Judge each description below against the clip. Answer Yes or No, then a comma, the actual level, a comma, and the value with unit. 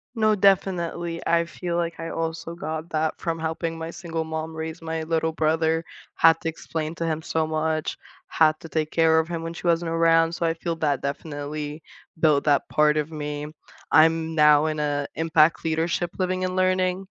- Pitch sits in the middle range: Yes, medium, 160 Hz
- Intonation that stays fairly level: Yes, narrow, 1.2 semitones